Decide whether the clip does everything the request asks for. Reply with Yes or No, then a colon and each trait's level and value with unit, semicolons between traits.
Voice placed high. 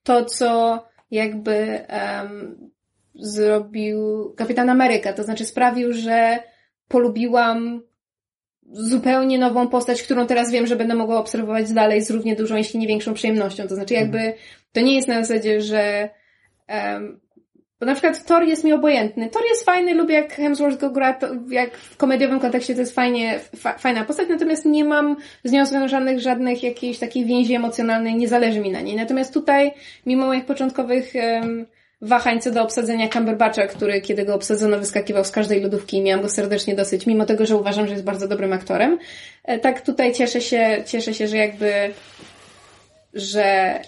Yes: high, 235 Hz